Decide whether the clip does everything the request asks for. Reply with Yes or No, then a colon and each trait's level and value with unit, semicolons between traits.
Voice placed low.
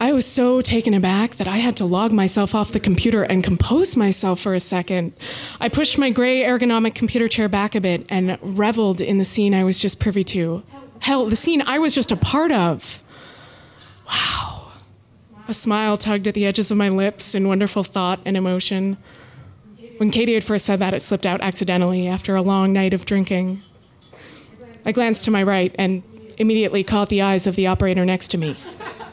No: high, 200 Hz